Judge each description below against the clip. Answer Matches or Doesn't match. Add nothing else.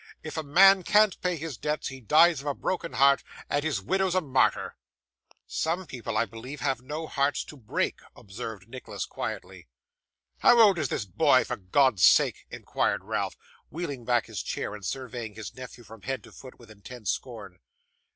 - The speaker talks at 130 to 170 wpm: Doesn't match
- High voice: Doesn't match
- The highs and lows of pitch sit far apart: Matches